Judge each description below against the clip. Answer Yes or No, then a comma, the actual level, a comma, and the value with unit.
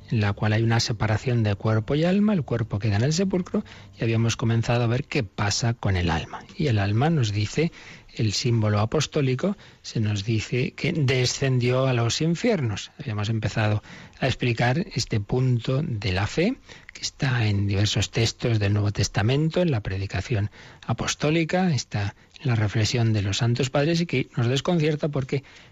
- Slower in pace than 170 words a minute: No, average, 175 wpm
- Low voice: Yes, low, 120 Hz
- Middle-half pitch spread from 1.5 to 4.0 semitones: No, average, 5.1 semitones